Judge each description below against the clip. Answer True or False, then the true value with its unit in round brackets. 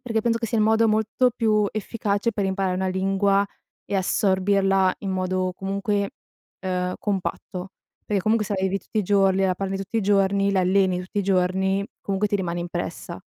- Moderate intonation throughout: False (1.6 semitones)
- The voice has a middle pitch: False (195 Hz)